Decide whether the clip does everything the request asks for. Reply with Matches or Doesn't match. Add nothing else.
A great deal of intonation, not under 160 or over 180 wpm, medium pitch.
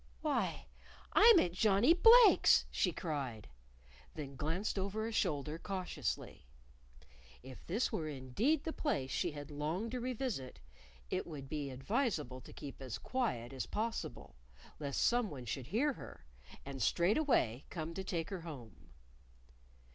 Doesn't match